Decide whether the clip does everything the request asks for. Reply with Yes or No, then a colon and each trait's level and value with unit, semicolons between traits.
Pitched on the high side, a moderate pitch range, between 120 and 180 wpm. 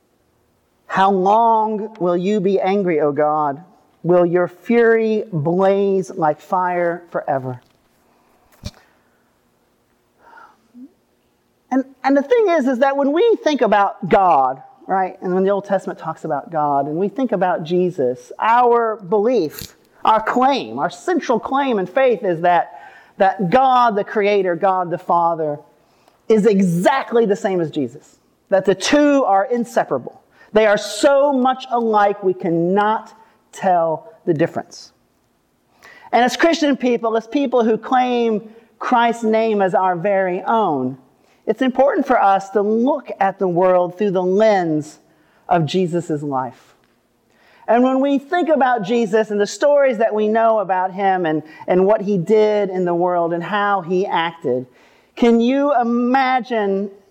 Yes: high, 205 Hz; average, 5.0 semitones; average, 145 wpm